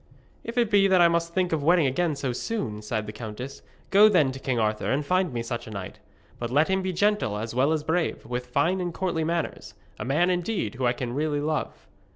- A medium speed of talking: No, fast, 235 wpm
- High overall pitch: No, medium, 155 Hz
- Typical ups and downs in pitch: No, wide, 6.5 semitones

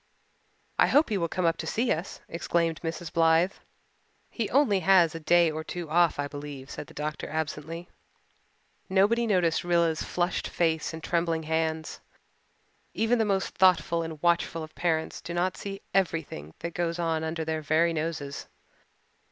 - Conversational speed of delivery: Yes, average, 165 wpm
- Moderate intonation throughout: No, narrow, 1.9 semitones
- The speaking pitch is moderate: Yes, medium, 165 Hz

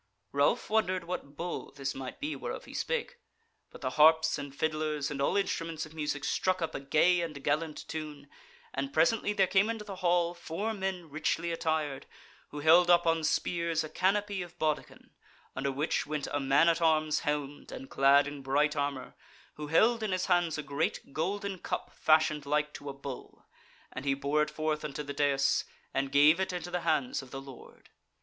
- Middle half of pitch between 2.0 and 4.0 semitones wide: Yes, average, 3.6 semitones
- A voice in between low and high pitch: Yes, medium, 155 Hz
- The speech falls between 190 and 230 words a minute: Yes, average, 195 wpm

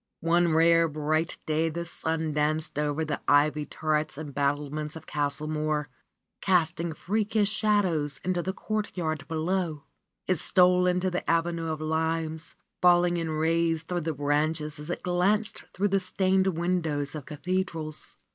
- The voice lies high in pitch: No, medium, 160 Hz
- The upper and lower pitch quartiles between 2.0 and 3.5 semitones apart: Yes, average, 2.8 semitones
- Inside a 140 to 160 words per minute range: Yes, average, 145 wpm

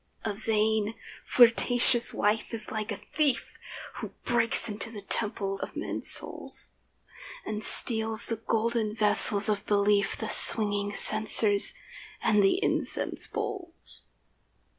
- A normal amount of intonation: No, narrow, 1.7 semitones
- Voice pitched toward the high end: Yes, high, 215 Hz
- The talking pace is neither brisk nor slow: No, slow, 120 wpm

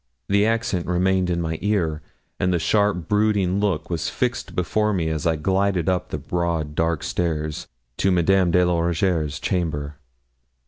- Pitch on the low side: Yes, very low, 90 Hz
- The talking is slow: No, average, 165 wpm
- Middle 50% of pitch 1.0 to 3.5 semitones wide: Yes, average, 3.1 semitones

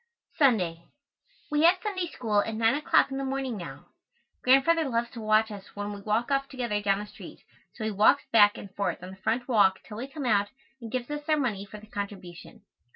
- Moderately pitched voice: No, high, 225 Hz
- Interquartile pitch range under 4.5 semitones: No, average, 4.8 semitones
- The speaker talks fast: Yes, fast, 220 wpm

